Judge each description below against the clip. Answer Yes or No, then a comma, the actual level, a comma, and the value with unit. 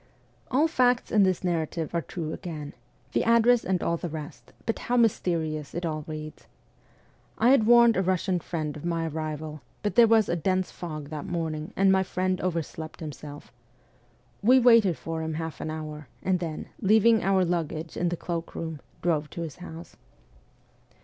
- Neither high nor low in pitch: Yes, medium, 170 Hz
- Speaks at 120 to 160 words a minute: No, average, 175 wpm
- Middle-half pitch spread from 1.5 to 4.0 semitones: Yes, average, 3.6 semitones